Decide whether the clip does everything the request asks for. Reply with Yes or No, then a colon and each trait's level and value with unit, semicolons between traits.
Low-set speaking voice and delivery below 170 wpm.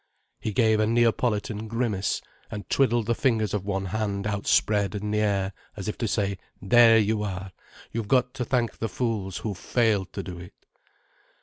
No: low, 105 Hz; average, 180 wpm